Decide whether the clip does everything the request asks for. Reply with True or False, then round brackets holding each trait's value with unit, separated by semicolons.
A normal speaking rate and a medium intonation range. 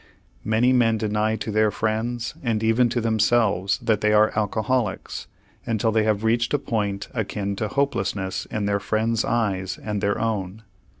False (165 wpm; 1.9 semitones)